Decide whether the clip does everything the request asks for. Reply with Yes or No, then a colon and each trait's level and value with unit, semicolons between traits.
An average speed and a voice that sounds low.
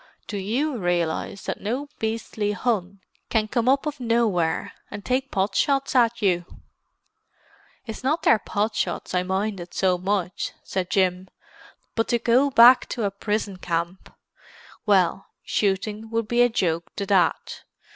No: average, 150 wpm; high, 210 Hz